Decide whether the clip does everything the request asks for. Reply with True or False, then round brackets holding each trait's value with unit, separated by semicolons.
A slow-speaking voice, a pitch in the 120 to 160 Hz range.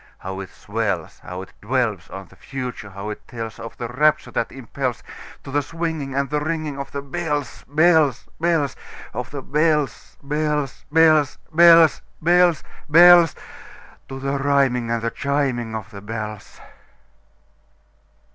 True (125 wpm; 140 Hz)